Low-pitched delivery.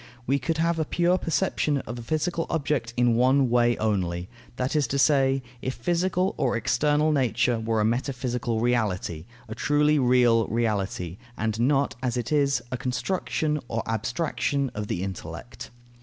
Yes: low, 125 Hz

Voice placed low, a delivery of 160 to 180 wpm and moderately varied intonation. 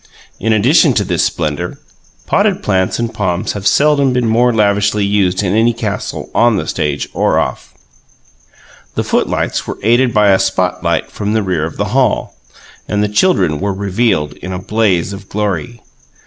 Yes: low, 105 Hz; average, 175 wpm; average, 3.4 semitones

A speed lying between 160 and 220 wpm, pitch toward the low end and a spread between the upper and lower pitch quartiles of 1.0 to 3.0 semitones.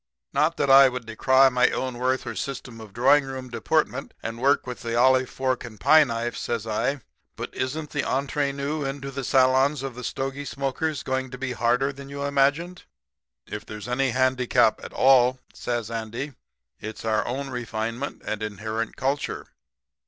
Yes: average, 175 wpm; low, 130 Hz; narrow, 2.6 semitones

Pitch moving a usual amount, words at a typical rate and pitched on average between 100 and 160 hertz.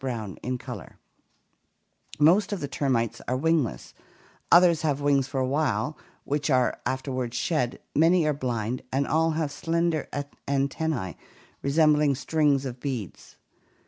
No: average, 3.5 semitones; slow, 130 wpm; medium, 140 Hz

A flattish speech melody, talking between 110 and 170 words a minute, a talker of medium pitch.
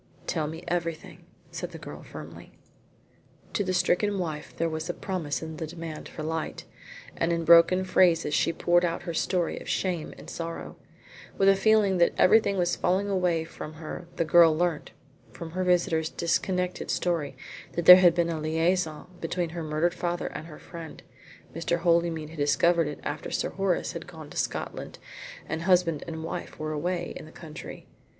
No: narrow, 2.0 semitones; average, 180 wpm; medium, 170 Hz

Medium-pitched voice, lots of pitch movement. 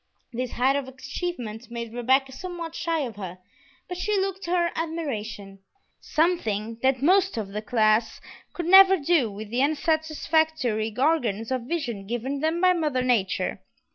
No: very high, 265 Hz; wide, 6.6 semitones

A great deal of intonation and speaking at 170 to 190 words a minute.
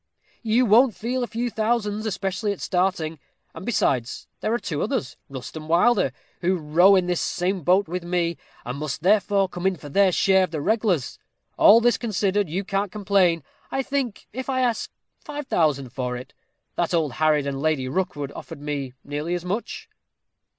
Yes: wide, 5.7 semitones; average, 180 wpm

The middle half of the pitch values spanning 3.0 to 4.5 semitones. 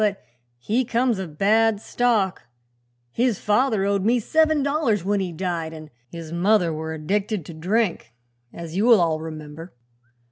No: wide, 5.5 semitones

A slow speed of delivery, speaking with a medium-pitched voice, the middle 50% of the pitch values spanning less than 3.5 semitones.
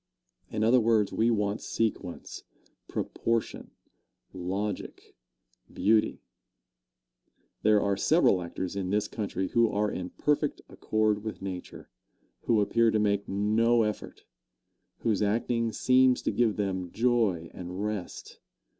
No: slow, 120 wpm; low, 105 Hz; average, 2.8 semitones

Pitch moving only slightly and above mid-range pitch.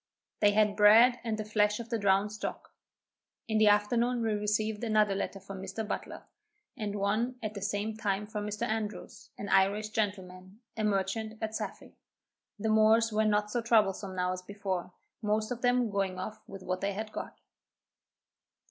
Yes: narrow, 1.7 semitones; high, 210 Hz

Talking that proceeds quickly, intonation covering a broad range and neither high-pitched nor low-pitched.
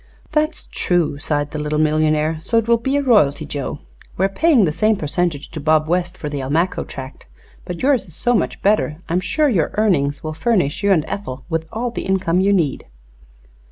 Yes: fast, 215 wpm; wide, 5.8 semitones; medium, 170 Hz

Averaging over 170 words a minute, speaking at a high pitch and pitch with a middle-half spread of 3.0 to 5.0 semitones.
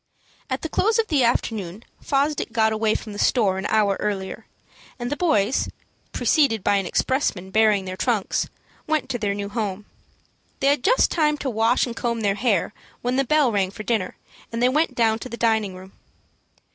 Yes: average, 195 wpm; high, 225 Hz; average, 4.4 semitones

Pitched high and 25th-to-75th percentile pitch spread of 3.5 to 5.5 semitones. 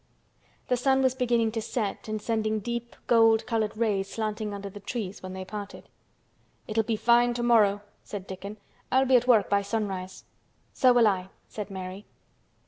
No: high, 215 Hz; average, 2.9 semitones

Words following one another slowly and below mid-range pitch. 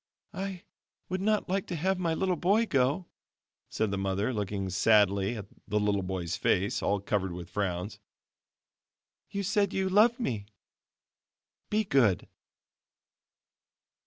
Yes: slow, 130 wpm; low, 110 Hz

